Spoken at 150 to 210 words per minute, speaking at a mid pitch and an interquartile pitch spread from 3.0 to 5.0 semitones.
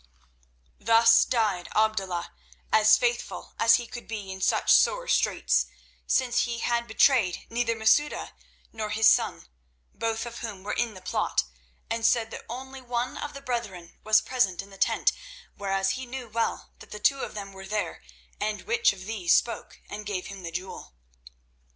No: average, 175 wpm; high, 225 Hz; average, 3.3 semitones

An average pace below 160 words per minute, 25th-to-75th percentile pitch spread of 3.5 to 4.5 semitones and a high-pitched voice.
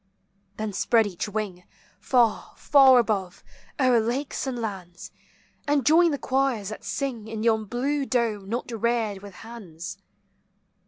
Yes: average, 140 wpm; average, 4.0 semitones; high, 230 Hz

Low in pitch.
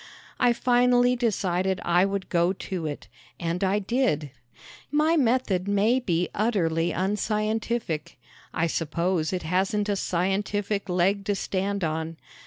No: high, 195 Hz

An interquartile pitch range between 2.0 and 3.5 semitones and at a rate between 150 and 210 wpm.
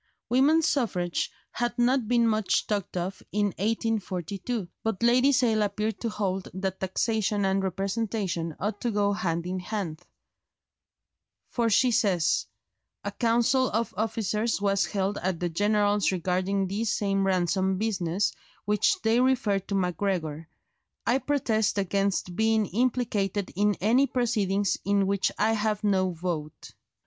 No: average, 3.0 semitones; slow, 135 wpm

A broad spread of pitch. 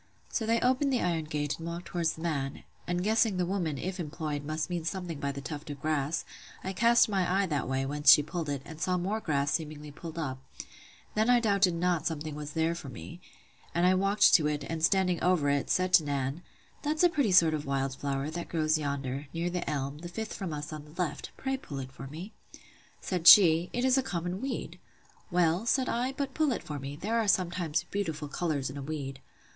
No: average, 4.3 semitones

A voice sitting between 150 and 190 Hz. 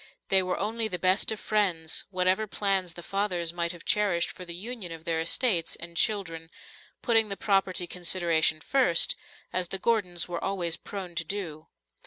Yes: medium, 185 Hz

